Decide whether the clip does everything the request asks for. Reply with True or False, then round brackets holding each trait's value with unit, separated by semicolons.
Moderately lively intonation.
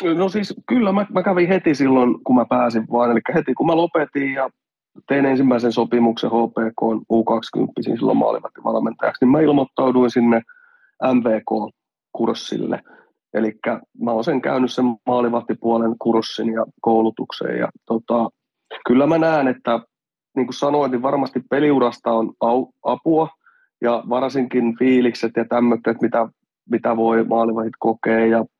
True (3.4 semitones)